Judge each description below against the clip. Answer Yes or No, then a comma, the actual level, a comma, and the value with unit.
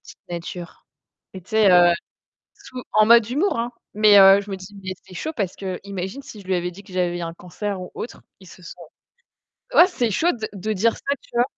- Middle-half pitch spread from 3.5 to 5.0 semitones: Yes, average, 3.8 semitones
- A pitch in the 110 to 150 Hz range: No, high, 200 Hz